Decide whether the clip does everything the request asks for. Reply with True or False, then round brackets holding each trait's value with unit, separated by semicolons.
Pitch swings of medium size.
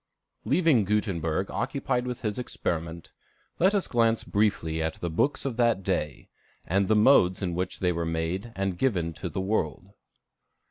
False (5.7 semitones)